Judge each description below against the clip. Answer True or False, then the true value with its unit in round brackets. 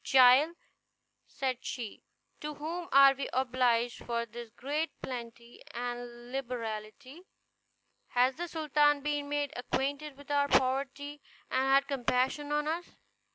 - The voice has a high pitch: True (270 Hz)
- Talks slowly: True (125 wpm)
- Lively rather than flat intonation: False (3.1 semitones)